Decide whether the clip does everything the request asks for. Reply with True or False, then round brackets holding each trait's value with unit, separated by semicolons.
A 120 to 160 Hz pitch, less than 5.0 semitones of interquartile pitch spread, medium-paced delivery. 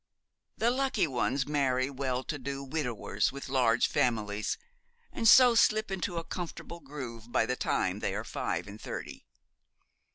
False (135 Hz; 5.5 semitones; 155 wpm)